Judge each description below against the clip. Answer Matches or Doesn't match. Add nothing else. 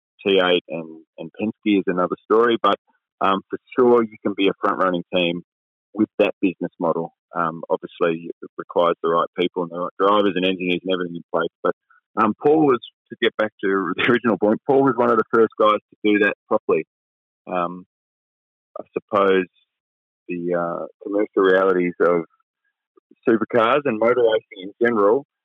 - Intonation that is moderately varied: Matches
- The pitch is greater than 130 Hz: Doesn't match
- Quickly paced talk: Doesn't match